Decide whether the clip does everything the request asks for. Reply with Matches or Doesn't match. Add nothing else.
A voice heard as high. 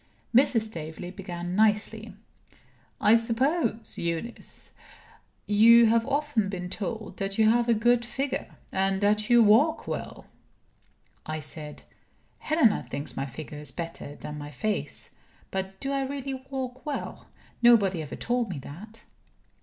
Matches